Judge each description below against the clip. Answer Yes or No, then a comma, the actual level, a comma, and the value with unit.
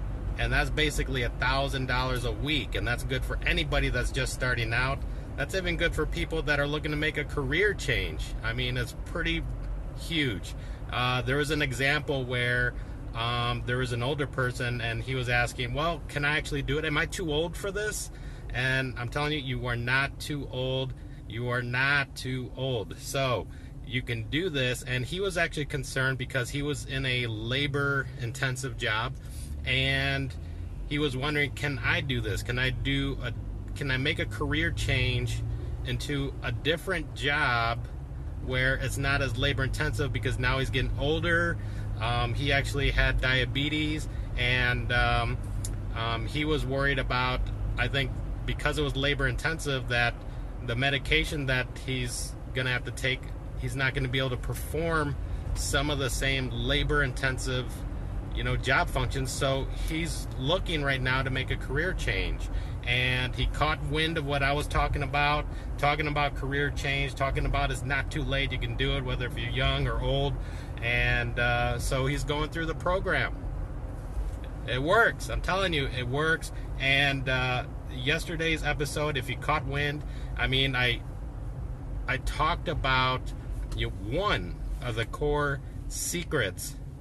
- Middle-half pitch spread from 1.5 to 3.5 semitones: Yes, average, 2.8 semitones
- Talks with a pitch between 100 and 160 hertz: Yes, low, 130 Hz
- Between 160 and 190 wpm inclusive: Yes, average, 170 wpm